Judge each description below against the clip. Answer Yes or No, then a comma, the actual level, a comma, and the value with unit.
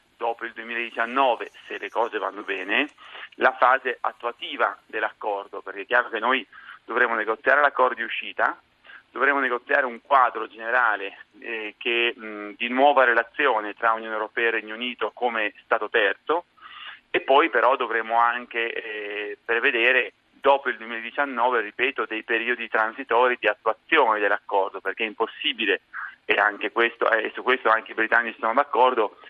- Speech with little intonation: Yes, narrow, 1.6 semitones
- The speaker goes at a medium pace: Yes, average, 150 wpm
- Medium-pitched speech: No, low, 115 Hz